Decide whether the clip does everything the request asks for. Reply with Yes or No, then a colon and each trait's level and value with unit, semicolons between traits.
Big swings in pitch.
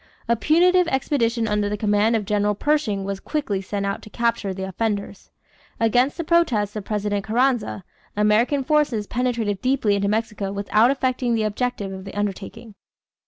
No: average, 3.4 semitones